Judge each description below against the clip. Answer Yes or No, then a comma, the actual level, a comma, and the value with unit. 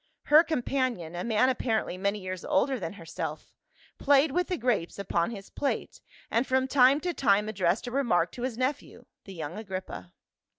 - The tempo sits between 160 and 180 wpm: Yes, average, 175 wpm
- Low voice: No, high, 230 Hz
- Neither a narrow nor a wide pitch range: No, wide, 5.9 semitones